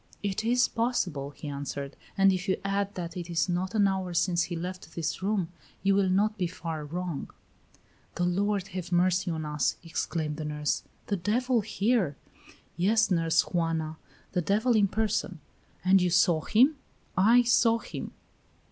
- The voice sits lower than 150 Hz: No, medium, 185 Hz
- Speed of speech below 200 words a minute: Yes, average, 165 wpm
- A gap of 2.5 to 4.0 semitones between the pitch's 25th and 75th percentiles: Yes, average, 3.6 semitones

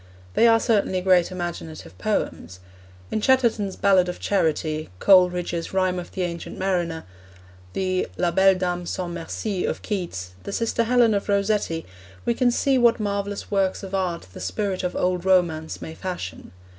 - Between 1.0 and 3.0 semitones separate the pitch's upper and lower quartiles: Yes, narrow, 2.6 semitones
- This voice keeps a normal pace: Yes, average, 160 wpm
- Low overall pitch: No, medium, 185 Hz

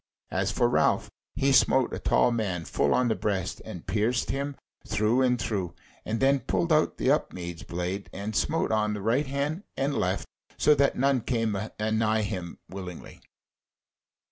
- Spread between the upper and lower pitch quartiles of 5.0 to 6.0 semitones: Yes, wide, 5.4 semitones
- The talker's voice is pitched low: Yes, low, 110 Hz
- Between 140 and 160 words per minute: No, average, 170 wpm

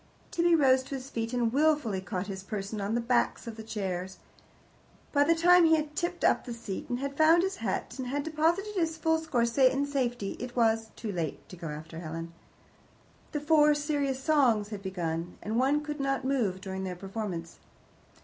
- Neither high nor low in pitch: No, high, 245 Hz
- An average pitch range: No, wide, 7.2 semitones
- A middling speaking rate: Yes, average, 195 wpm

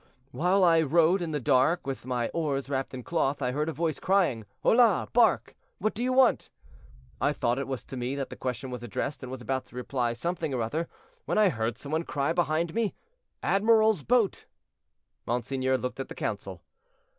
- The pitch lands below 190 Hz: Yes, medium, 140 Hz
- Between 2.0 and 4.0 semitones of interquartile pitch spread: No, wide, 5.6 semitones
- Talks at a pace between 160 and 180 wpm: No, average, 200 wpm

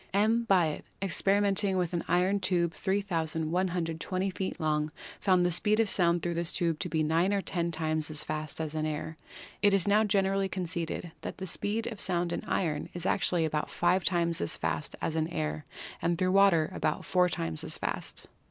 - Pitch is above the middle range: No, medium, 175 Hz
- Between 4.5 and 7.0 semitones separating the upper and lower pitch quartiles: No, average, 3.2 semitones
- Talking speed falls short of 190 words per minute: No, average, 195 wpm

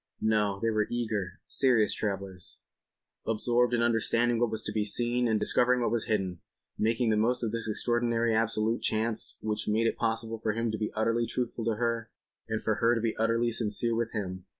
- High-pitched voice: No, low, 115 Hz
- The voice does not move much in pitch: Yes, narrow, 1.6 semitones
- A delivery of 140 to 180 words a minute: No, average, 195 wpm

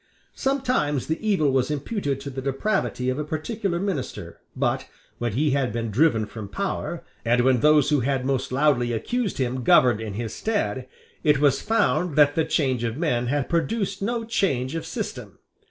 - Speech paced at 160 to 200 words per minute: Yes, average, 180 wpm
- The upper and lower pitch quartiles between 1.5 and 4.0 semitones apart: No, wide, 5.4 semitones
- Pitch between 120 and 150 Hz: Yes, medium, 140 Hz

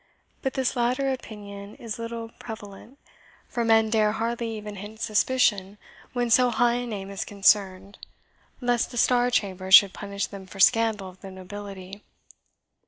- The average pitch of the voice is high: Yes, high, 215 Hz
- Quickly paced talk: No, average, 155 wpm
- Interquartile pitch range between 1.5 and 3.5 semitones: Yes, average, 3.1 semitones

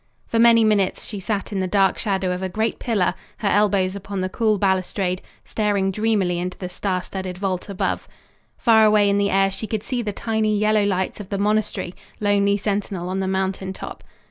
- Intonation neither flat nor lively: No, narrow, 2.1 semitones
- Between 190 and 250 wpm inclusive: Yes, average, 200 wpm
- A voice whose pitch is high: Yes, high, 200 Hz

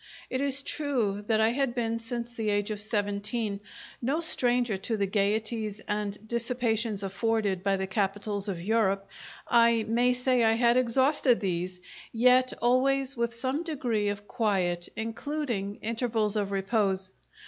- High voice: Yes, high, 225 Hz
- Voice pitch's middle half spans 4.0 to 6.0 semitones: No, average, 3.3 semitones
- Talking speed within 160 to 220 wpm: No, average, 150 wpm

